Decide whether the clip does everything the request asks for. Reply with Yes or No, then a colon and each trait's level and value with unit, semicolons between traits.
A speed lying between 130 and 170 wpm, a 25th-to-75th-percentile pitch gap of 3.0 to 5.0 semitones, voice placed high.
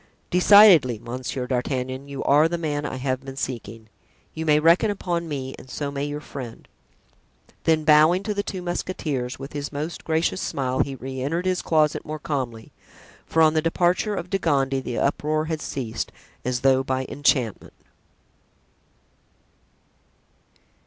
No: average, 155 wpm; average, 3.8 semitones; medium, 145 Hz